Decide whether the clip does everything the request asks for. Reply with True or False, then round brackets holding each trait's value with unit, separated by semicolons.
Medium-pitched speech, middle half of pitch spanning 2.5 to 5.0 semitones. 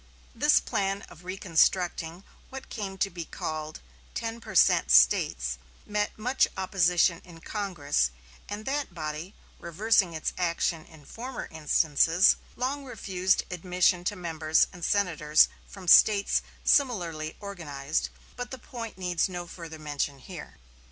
True (180 Hz; 4.2 semitones)